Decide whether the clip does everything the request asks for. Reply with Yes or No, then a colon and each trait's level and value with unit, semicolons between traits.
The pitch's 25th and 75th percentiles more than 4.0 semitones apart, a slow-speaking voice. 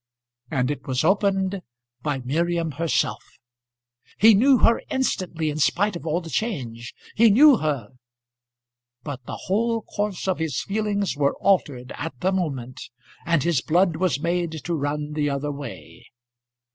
No: wide, 5.4 semitones; average, 150 wpm